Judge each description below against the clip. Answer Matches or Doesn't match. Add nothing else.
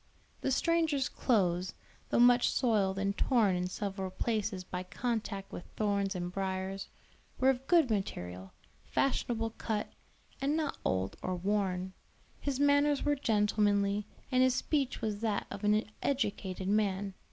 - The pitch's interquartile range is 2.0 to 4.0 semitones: Doesn't match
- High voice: Matches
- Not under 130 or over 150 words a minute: Matches